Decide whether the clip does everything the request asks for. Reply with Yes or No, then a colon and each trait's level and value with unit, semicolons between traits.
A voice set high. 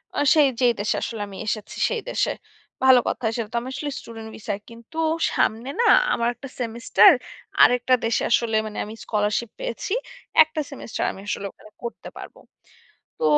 Yes: high, 235 Hz